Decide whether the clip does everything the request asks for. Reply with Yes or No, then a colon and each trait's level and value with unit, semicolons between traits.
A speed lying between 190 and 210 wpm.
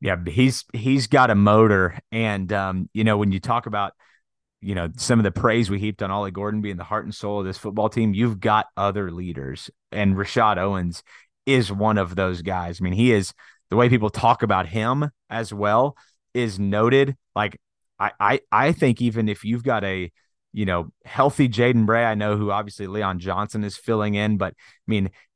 Yes: fast, 205 wpm